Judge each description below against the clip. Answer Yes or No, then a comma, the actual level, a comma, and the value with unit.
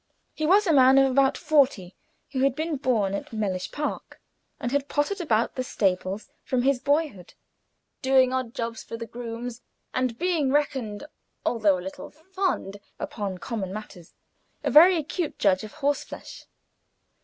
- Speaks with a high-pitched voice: Yes, very high, 255 Hz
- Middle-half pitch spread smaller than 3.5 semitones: No, average, 5.3 semitones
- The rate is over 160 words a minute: No, average, 155 wpm